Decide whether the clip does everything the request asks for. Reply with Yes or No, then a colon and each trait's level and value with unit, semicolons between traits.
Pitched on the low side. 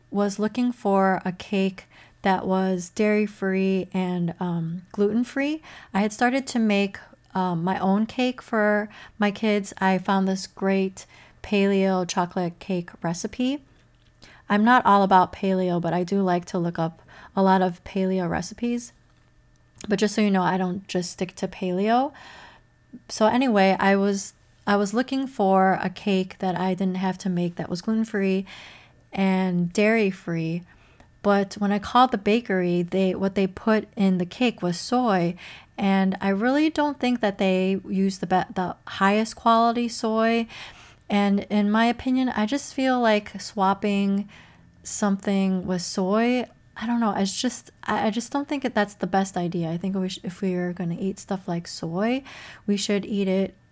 No: high, 195 Hz